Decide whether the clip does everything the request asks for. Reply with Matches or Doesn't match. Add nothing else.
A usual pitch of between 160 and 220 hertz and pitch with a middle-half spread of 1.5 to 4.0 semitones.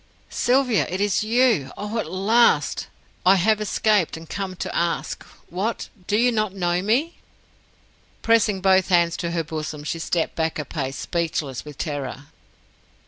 Doesn't match